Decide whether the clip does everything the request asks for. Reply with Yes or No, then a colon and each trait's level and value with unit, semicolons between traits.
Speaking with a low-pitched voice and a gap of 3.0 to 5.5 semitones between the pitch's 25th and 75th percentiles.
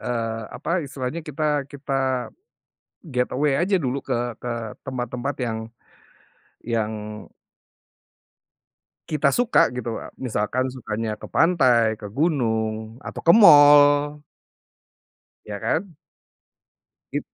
Yes: low, 130 Hz; average, 4.2 semitones